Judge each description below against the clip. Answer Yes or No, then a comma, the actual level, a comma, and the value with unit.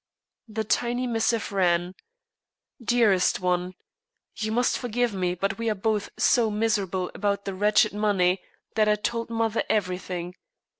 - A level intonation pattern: No, average, 3.5 semitones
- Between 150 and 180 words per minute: No, average, 140 wpm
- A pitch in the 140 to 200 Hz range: No, high, 210 Hz